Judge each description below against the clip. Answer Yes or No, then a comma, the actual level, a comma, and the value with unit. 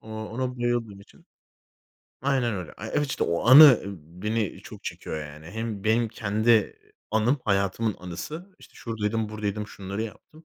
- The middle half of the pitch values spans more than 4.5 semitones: No, average, 3.1 semitones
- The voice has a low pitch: Yes, low, 110 Hz